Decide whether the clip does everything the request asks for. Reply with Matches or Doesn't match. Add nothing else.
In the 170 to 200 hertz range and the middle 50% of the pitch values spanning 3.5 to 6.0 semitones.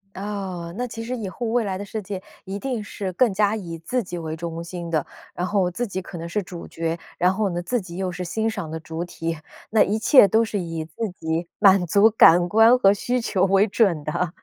Matches